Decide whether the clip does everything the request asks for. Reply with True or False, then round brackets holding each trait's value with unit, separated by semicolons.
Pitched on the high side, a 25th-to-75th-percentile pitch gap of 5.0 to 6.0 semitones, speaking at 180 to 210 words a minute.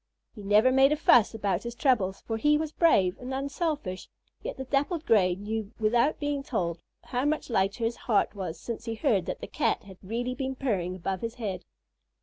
True (230 Hz; 5.4 semitones; 200 wpm)